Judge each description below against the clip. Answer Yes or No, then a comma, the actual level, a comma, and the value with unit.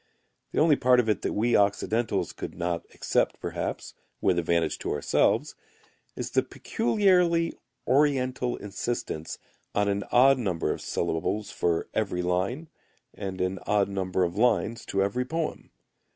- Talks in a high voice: No, low, 105 Hz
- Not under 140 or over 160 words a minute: Yes, average, 145 wpm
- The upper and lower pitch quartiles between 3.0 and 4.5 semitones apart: No, wide, 5.5 semitones